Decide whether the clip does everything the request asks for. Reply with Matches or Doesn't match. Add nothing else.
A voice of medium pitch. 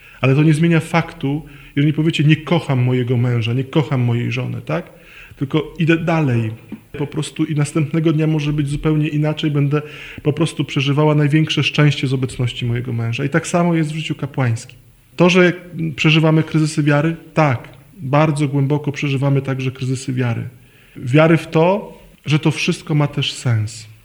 Matches